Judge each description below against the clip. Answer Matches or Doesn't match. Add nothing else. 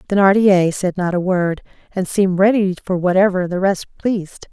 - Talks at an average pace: Matches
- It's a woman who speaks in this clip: Matches